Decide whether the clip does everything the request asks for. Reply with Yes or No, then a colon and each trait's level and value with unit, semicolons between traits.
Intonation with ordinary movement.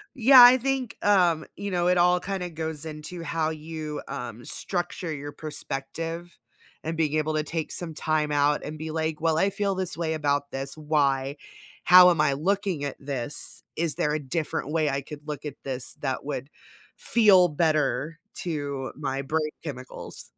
Yes: average, 3.3 semitones